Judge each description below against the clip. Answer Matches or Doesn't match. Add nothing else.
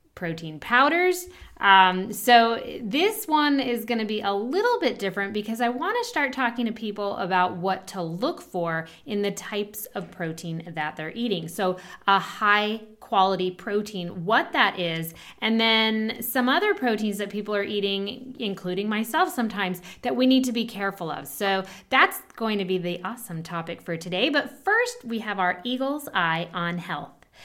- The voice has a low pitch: Doesn't match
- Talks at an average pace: Matches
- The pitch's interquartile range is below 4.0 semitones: Doesn't match